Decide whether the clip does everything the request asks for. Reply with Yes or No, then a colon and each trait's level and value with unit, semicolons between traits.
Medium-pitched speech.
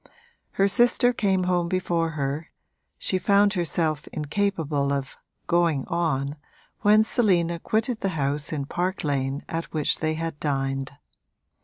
Yes: medium, 165 Hz